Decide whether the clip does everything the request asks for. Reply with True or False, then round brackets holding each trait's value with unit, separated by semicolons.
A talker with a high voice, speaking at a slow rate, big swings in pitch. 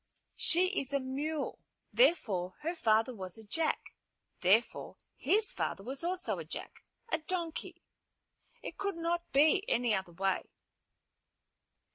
True (280 Hz; 130 wpm; 7.8 semitones)